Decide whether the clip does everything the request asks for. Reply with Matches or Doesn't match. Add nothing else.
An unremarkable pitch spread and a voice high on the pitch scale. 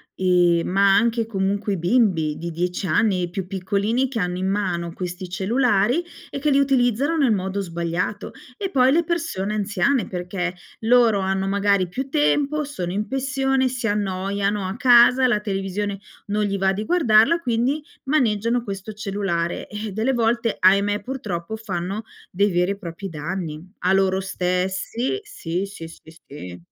Matches